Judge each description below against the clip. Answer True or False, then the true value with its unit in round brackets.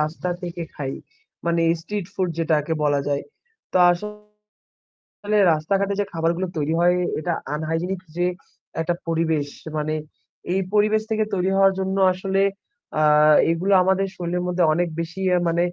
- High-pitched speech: False (175 Hz)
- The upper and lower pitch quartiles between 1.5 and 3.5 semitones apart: True (2.9 semitones)